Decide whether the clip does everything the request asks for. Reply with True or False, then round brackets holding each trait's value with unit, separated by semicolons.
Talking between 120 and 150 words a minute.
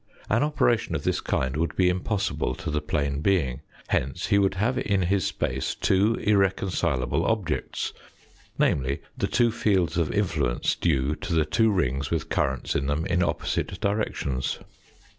False (160 wpm)